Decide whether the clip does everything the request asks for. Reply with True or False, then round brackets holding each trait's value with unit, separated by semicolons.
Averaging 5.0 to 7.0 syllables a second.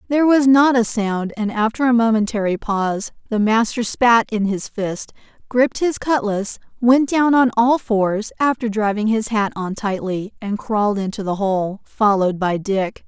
False (4.6 syllables/s)